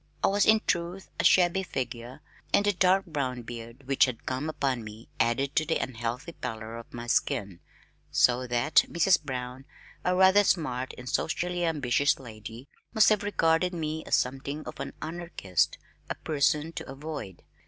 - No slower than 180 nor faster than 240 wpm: No, average, 165 wpm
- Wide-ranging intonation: Yes, wide, 5.9 semitones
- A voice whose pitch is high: No, medium, 140 Hz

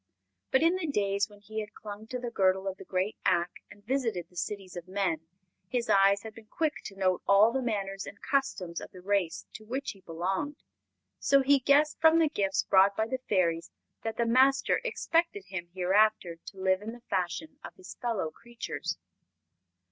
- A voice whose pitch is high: Yes, high, 205 Hz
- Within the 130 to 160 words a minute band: No, average, 195 wpm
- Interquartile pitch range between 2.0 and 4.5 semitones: No, wide, 5.4 semitones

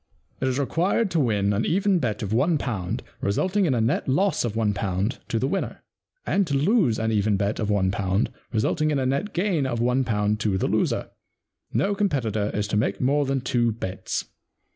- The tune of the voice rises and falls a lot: Yes, wide, 6.4 semitones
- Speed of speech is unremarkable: No, fast, 210 wpm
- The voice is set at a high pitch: No, low, 120 Hz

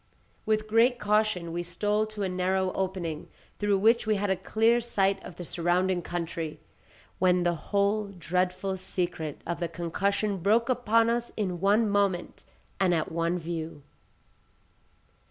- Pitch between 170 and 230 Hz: Yes, high, 190 Hz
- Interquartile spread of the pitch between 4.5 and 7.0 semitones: No, average, 3.4 semitones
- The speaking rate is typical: Yes, average, 150 wpm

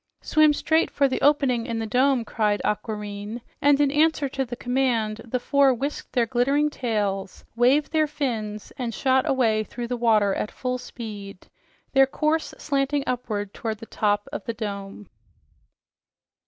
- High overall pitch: Yes, high, 245 Hz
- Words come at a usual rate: Yes, average, 160 wpm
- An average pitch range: Yes, average, 4.3 semitones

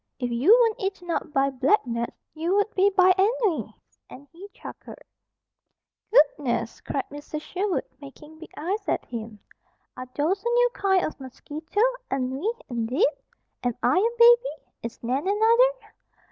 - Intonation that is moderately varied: No, wide, 7.5 semitones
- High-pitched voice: Yes, very high, 335 Hz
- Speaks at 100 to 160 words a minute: Yes, average, 150 wpm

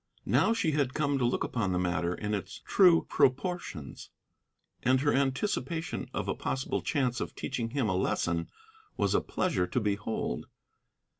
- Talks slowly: No, average, 160 wpm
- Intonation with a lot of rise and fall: Yes, wide, 6.6 semitones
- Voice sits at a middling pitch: No, low, 130 Hz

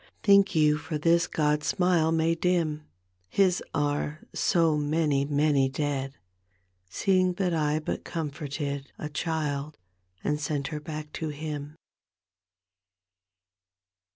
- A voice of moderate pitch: Yes, medium, 150 Hz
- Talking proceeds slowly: Yes, slow, 120 wpm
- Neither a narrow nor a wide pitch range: No, narrow, 2.1 semitones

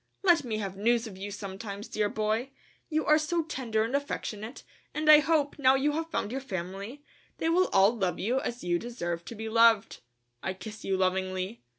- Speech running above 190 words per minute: Yes, average, 200 wpm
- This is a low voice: No, high, 225 Hz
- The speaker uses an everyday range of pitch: No, wide, 6.1 semitones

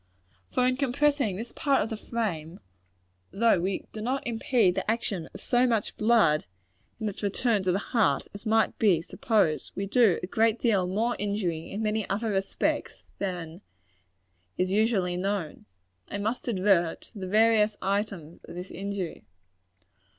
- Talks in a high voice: Yes, high, 205 Hz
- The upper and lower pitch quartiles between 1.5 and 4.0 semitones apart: Yes, average, 3.6 semitones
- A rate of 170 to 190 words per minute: No, average, 160 wpm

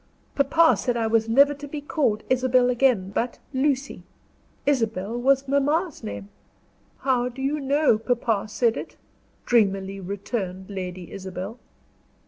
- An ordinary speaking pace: No, slow, 130 wpm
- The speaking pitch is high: Yes, high, 240 Hz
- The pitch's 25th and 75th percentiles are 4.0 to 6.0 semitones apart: Yes, wide, 5.5 semitones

